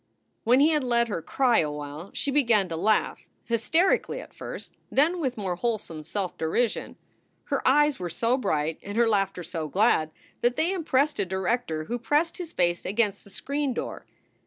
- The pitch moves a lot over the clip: Yes, wide, 7.4 semitones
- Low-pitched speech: No, high, 230 Hz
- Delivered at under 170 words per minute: No, average, 180 wpm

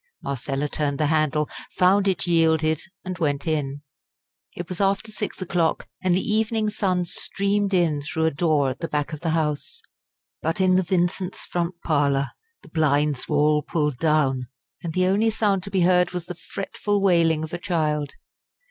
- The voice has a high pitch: No, medium, 165 Hz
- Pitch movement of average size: Yes, average, 3.7 semitones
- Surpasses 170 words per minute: Yes, average, 180 wpm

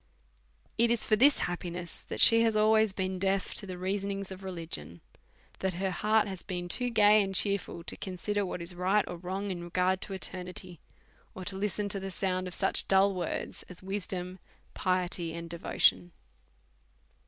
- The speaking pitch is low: No, high, 190 Hz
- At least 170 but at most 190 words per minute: Yes, average, 175 wpm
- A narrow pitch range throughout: Yes, narrow, 2.0 semitones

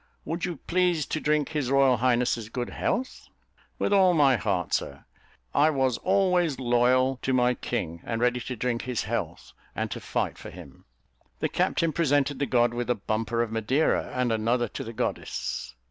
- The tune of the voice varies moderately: Yes, average, 3.9 semitones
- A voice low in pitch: Yes, low, 125 Hz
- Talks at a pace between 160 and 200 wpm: Yes, average, 180 wpm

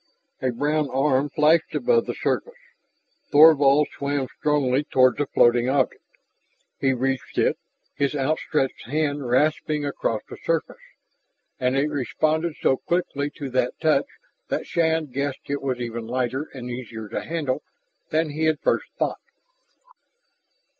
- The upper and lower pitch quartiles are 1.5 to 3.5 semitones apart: Yes, average, 3.0 semitones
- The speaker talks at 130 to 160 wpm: Yes, average, 140 wpm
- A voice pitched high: No, medium, 140 Hz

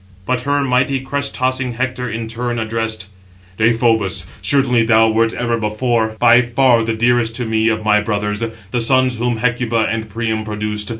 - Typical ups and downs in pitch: No, narrow, 2.1 semitones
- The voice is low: Yes, low, 115 Hz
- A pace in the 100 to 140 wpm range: No, average, 170 wpm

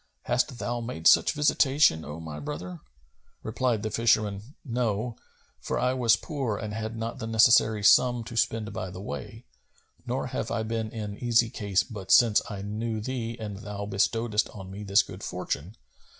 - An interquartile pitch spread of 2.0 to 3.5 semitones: Yes, narrow, 2.6 semitones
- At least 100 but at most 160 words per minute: No, average, 175 wpm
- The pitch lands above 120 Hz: No, low, 110 Hz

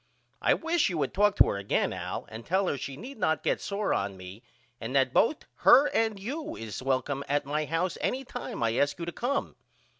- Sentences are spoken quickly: Yes, fast, 220 wpm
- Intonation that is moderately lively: No, wide, 8.8 semitones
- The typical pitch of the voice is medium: Yes, medium, 160 Hz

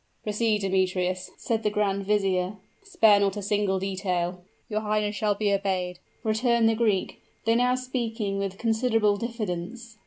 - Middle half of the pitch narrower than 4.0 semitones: Yes, average, 2.7 semitones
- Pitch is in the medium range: No, high, 210 Hz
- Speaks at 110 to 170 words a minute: Yes, average, 150 wpm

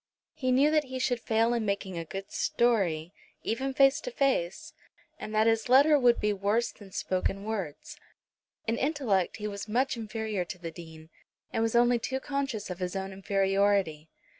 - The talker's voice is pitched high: Yes, high, 215 Hz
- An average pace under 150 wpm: No, average, 180 wpm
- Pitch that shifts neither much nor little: Yes, average, 4.7 semitones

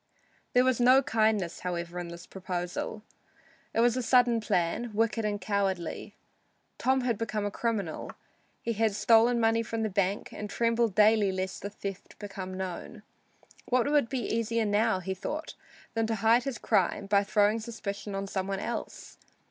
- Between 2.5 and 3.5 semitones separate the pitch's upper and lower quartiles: Yes, average, 3.0 semitones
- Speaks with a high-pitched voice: Yes, high, 215 Hz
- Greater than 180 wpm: No, average, 170 wpm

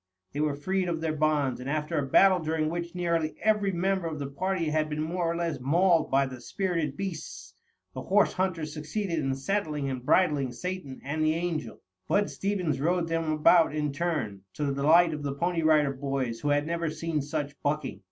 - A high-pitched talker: No, medium, 155 Hz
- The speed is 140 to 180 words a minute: No, average, 200 wpm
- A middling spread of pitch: Yes, average, 3.3 semitones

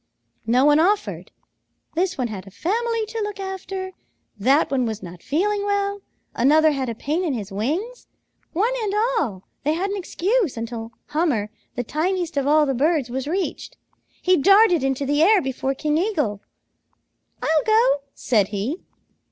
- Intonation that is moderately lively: No, wide, 7.5 semitones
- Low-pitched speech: No, very high, 310 Hz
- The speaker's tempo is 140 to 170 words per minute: Yes, average, 165 wpm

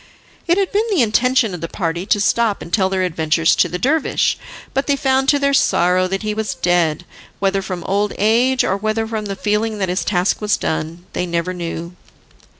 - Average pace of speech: No, fast, 210 wpm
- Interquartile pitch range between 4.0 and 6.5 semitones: Yes, average, 4.5 semitones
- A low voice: No, high, 200 Hz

